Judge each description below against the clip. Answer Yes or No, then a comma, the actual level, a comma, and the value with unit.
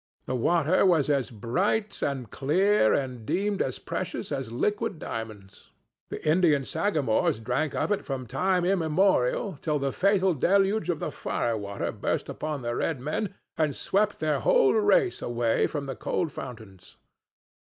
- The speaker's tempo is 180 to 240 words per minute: No, average, 150 wpm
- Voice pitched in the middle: Yes, medium, 150 Hz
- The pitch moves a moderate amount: No, wide, 7.5 semitones